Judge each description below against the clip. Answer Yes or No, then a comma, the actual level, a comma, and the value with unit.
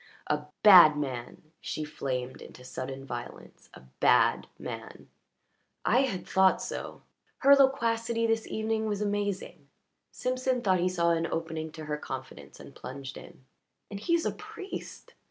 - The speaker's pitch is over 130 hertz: Yes, medium, 185 Hz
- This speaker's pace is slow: No, average, 150 wpm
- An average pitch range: No, wide, 7.3 semitones